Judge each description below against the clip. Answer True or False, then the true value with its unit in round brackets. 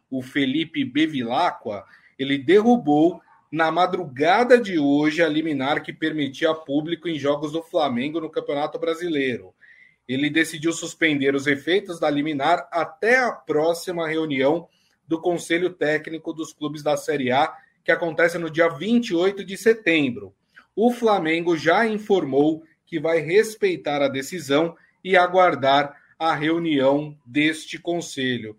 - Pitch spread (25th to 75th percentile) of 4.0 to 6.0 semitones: False (3.5 semitones)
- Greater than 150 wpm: False (130 wpm)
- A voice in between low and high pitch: True (165 Hz)